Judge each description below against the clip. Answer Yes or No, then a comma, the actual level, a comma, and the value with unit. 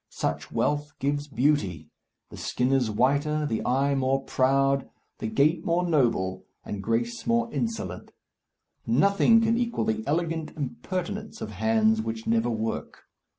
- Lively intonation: Yes, wide, 7.1 semitones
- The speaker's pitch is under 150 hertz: Yes, medium, 140 Hz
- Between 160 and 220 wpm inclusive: No, average, 140 wpm